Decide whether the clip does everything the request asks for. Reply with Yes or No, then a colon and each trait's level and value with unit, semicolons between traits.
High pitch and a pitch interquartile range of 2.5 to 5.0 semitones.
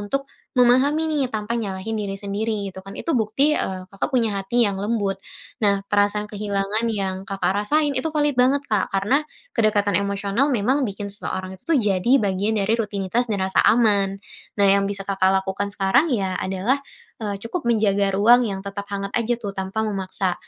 Yes: high, 205 Hz; average, 3.0 semitones